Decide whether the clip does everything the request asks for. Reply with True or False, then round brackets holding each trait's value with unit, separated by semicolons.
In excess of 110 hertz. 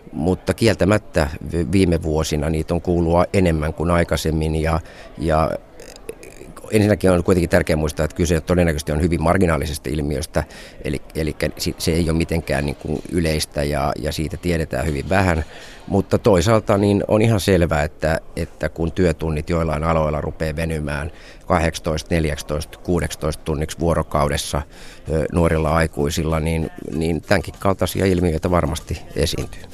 False (80 Hz)